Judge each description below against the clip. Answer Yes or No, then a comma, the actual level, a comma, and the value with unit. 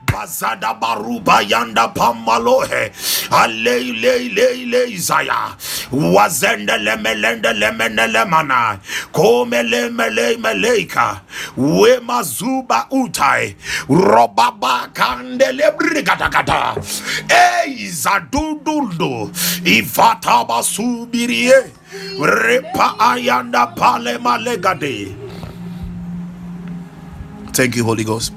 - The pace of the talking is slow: Yes, slow, 70 wpm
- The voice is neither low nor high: No, high, 195 Hz